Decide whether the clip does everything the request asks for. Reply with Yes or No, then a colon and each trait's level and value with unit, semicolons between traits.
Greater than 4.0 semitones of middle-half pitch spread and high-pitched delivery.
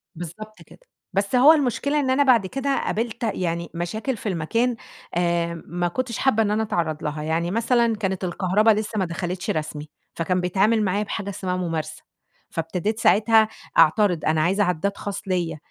Yes: average, 4.5 semitones; high, 195 Hz